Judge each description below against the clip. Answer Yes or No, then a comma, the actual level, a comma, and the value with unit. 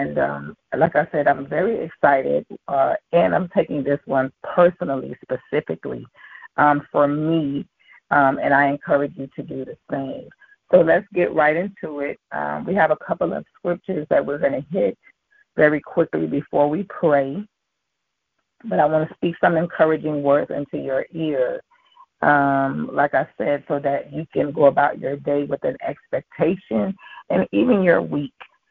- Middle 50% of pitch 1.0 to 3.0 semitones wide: No, average, 3.7 semitones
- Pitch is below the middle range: No, medium, 150 Hz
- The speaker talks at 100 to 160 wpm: No, average, 170 wpm